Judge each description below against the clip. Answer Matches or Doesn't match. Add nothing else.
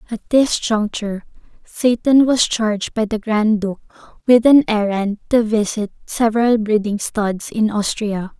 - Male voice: Doesn't match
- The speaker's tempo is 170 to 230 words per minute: Doesn't match